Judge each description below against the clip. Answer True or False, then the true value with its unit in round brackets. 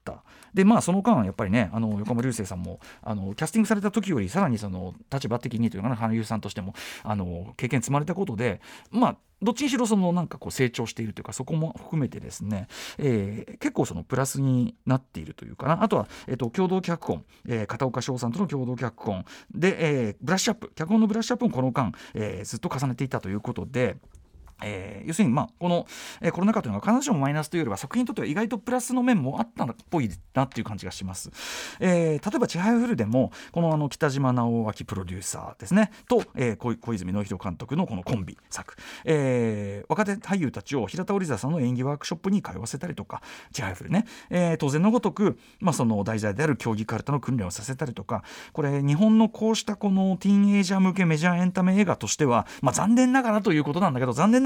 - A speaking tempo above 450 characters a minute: True (470 characters per minute)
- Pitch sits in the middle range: True (145 Hz)